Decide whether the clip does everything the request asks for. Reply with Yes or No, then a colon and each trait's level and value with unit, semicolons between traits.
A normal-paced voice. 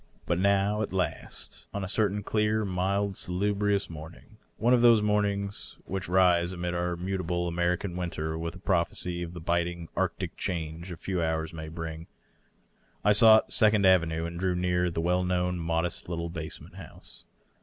Yes: average, 175 wpm